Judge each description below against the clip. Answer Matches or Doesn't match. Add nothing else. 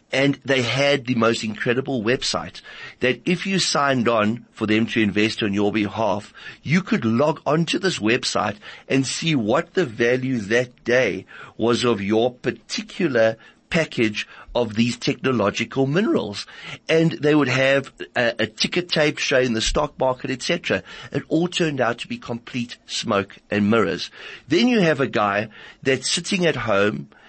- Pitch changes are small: Doesn't match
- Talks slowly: Doesn't match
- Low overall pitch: Matches